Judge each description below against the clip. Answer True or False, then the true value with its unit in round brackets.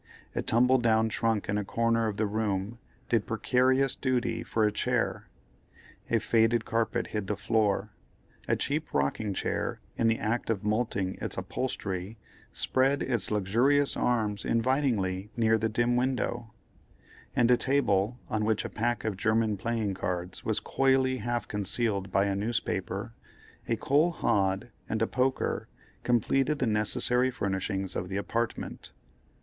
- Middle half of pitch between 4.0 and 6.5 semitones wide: False (3.1 semitones)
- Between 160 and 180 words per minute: False (150 wpm)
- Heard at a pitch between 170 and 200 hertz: False (110 Hz)